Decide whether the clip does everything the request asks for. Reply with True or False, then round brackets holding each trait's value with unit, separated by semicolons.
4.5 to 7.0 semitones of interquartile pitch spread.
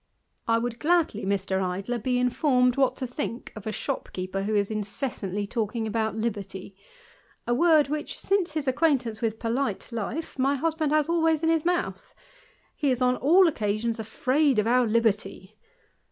True (5.5 semitones)